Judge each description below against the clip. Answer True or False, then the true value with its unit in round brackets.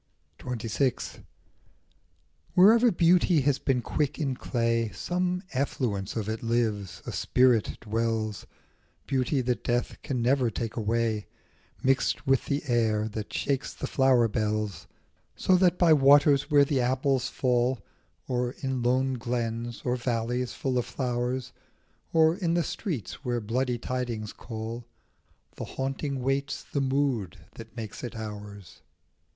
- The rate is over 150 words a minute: False (135 wpm)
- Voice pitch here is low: True (125 Hz)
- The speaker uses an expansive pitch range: False (3.2 semitones)